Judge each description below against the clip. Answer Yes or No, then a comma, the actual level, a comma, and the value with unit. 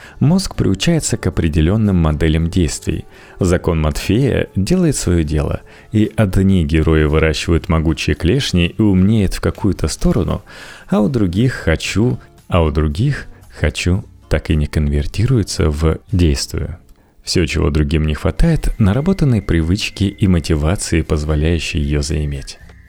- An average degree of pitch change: Yes, average, 4.4 semitones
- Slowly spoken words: No, average, 125 wpm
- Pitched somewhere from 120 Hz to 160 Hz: No, very low, 85 Hz